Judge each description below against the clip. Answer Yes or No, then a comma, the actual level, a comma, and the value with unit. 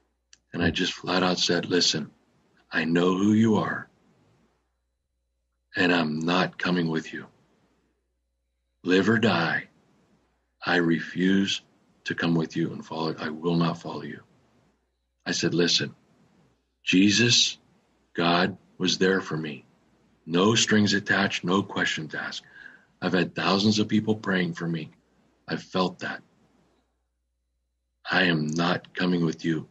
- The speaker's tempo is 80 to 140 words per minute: Yes, slow, 135 wpm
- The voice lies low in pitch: Yes, very low, 85 Hz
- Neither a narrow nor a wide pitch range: No, wide, 6.6 semitones